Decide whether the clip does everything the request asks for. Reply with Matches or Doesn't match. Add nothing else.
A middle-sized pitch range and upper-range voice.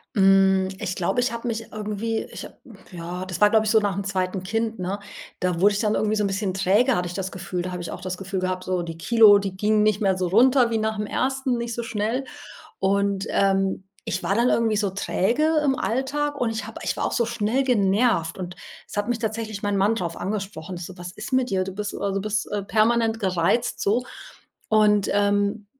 Matches